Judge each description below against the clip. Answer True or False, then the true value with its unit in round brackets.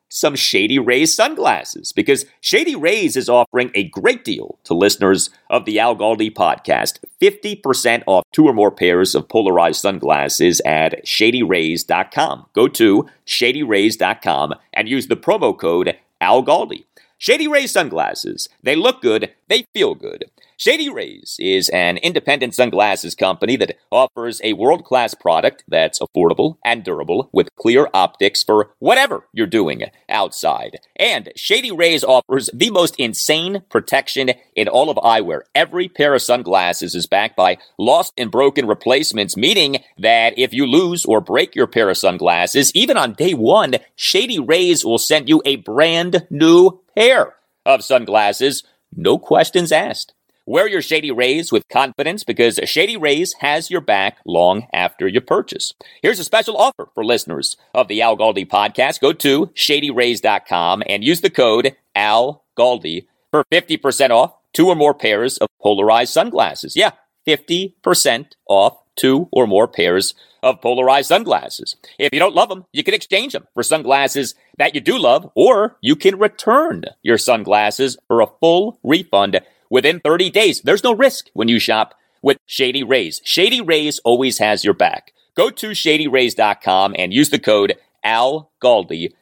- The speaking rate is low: False (155 wpm)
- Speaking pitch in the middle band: True (165 Hz)